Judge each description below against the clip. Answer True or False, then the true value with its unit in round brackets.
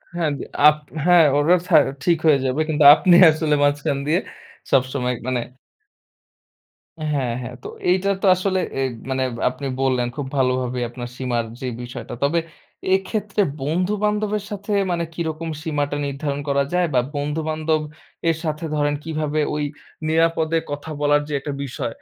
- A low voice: False (150 Hz)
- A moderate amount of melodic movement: True (3.4 semitones)